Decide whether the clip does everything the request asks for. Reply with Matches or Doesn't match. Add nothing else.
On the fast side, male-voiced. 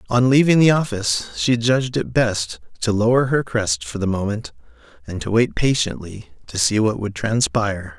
Doesn't match